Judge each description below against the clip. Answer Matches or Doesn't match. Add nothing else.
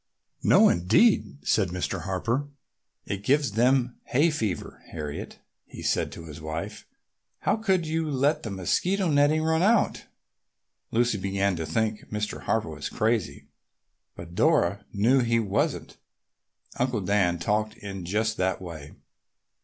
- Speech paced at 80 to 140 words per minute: Matches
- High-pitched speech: Doesn't match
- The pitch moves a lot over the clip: Matches